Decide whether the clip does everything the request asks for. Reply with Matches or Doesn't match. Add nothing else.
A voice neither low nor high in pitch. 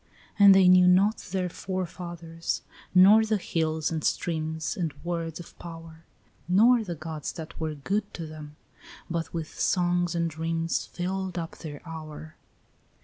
Matches